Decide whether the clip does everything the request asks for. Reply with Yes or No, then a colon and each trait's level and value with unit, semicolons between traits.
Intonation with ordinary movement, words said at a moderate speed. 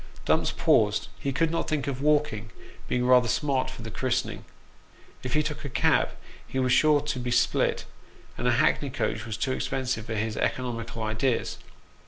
Yes: average, 3.4 semitones; average, 180 wpm